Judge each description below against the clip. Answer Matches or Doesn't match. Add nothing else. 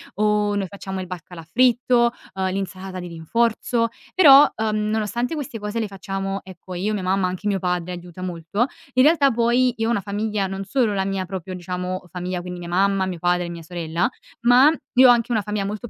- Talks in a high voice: Matches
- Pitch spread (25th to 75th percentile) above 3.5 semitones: Matches